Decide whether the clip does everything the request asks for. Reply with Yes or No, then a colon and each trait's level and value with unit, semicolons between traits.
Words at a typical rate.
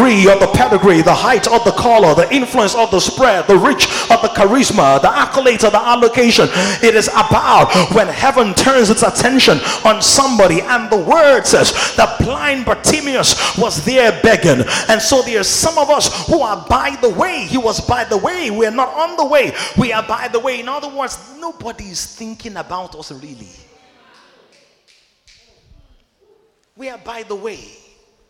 Yes: average, 180 wpm